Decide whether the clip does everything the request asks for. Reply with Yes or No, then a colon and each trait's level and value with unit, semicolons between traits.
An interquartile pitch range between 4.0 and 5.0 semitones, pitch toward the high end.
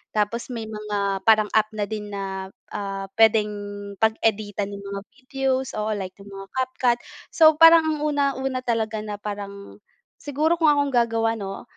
Yes: average, 4.3 semitones; high, 220 Hz